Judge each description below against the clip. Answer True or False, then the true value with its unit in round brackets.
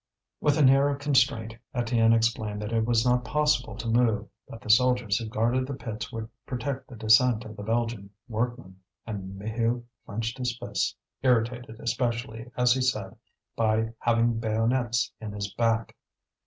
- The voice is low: True (115 Hz)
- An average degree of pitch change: False (2.0 semitones)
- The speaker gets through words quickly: False (165 wpm)